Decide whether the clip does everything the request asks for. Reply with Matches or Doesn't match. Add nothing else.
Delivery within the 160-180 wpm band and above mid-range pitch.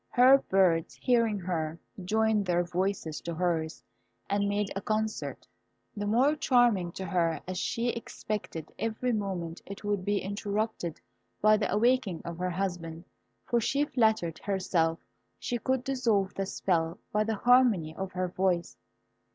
Doesn't match